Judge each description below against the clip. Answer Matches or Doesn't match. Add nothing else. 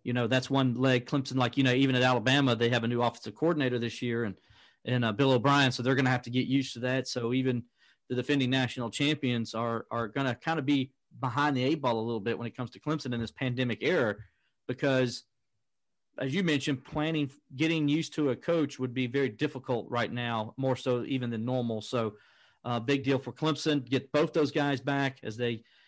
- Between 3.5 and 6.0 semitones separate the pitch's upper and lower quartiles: Doesn't match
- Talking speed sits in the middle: Doesn't match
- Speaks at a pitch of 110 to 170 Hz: Matches